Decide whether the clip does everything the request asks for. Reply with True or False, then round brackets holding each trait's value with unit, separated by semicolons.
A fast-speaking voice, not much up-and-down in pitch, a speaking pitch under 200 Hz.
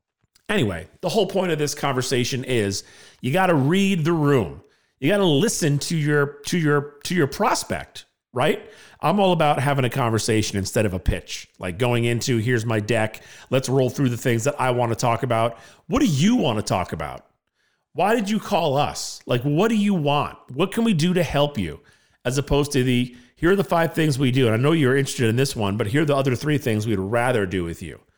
False (230 wpm; 5.1 semitones; 135 Hz)